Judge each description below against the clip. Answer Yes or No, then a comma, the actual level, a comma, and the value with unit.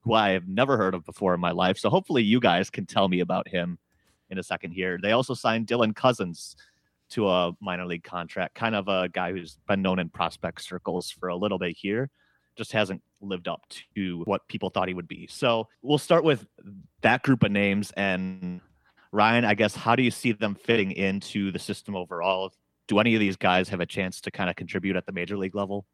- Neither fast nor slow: No, fast, 225 wpm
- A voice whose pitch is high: No, very low, 95 Hz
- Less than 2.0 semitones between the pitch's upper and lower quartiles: No, average, 2.9 semitones